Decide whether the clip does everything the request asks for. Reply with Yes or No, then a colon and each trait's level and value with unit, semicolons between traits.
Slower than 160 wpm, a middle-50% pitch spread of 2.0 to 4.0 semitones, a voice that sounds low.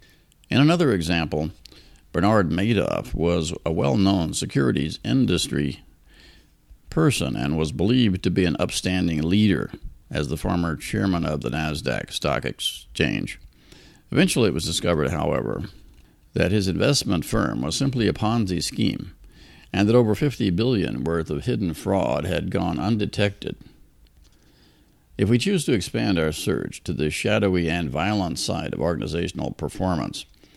No: average, 140 wpm; average, 4.9 semitones; very low, 85 Hz